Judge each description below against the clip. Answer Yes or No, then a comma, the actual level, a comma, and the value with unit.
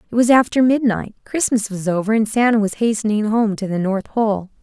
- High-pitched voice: Yes, high, 215 Hz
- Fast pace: Yes, fast, 210 wpm